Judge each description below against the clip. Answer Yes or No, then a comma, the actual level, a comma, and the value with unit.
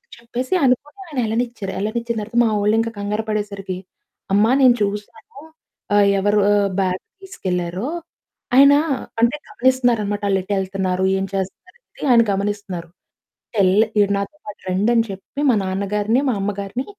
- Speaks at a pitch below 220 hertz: Yes, high, 210 Hz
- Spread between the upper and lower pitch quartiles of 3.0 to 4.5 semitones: Yes, average, 3.4 semitones